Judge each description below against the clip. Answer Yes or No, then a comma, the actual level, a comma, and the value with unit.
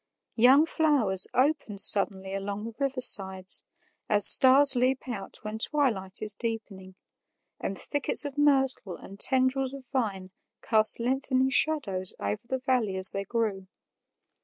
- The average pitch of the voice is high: Yes, high, 230 Hz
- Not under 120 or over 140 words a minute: Yes, slow, 135 wpm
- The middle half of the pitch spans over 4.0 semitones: Yes, average, 5.2 semitones